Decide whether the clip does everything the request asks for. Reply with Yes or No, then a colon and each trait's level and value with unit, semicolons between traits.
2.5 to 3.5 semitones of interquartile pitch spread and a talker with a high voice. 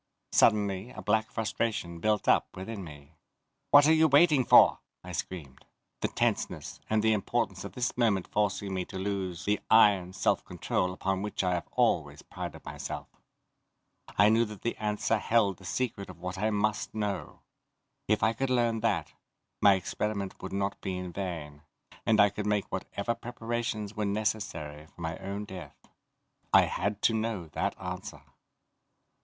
No: average, 3.0 semitones; low, 100 Hz